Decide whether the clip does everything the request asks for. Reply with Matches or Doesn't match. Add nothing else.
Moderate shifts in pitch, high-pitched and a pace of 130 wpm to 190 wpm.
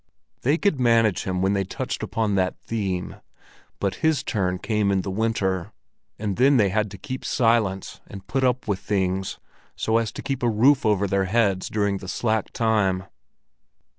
Doesn't match